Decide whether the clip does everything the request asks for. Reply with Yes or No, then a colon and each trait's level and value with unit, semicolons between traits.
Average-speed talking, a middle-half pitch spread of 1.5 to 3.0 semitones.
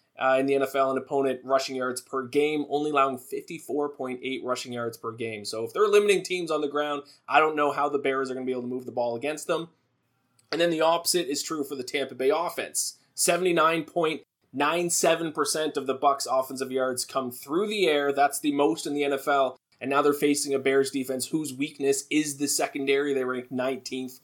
No: fast, 225 wpm; narrow, 2.5 semitones